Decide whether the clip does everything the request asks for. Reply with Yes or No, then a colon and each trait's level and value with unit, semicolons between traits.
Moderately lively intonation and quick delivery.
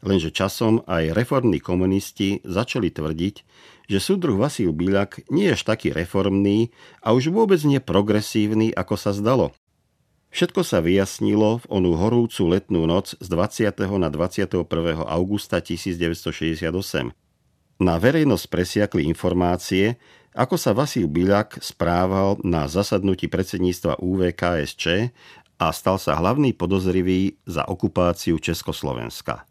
No: average, 3.1 semitones; average, 120 wpm